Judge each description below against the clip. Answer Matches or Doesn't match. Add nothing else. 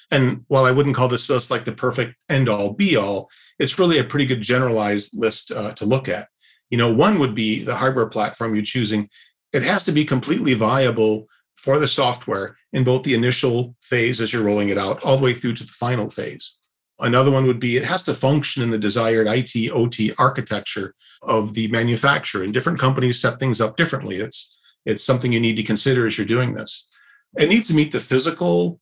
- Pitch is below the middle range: Matches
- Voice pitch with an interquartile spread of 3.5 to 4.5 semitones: Doesn't match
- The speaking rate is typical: Doesn't match